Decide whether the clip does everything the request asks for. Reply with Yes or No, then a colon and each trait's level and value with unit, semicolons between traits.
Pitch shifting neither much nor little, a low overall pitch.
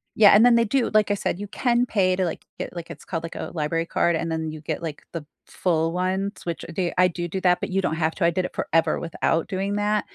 No: average, 3.4 semitones; medium, 180 Hz